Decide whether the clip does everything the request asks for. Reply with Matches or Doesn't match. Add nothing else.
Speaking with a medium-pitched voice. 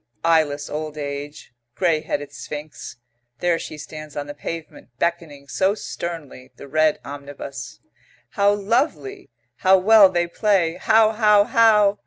Matches